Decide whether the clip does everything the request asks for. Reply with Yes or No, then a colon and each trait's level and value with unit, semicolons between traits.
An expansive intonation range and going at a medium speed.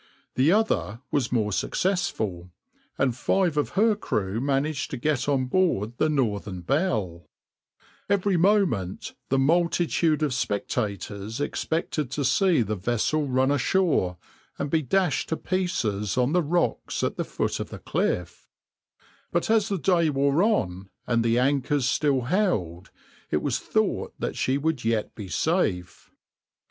Yes: wide, 7.6 semitones; average, 145 wpm